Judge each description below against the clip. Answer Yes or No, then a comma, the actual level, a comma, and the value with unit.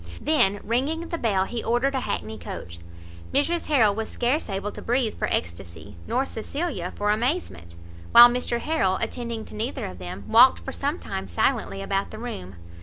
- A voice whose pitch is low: No, high, 225 Hz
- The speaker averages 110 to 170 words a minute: No, average, 180 wpm